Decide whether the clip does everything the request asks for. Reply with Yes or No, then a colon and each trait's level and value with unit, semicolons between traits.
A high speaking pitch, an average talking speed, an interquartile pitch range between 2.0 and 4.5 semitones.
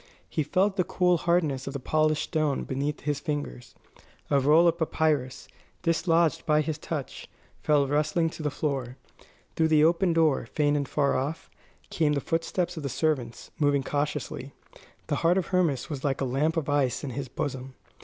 No: medium, 150 Hz; average, 180 wpm; average, 2.8 semitones